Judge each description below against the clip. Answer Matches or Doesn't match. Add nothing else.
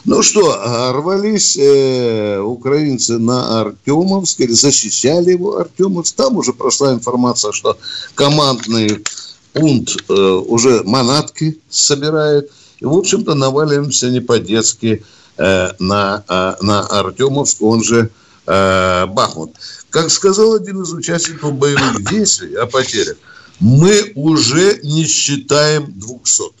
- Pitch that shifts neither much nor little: Doesn't match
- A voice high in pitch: Doesn't match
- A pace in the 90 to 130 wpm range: Matches